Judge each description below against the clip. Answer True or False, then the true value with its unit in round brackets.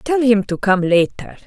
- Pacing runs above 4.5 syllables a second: False (4.4 syllables/s)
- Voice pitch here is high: True (210 Hz)